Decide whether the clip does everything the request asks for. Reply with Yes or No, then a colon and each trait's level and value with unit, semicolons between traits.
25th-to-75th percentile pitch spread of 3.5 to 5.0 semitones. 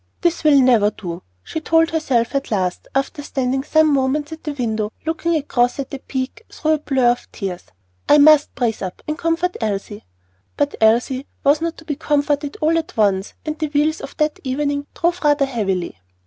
Yes: average, 4.3 semitones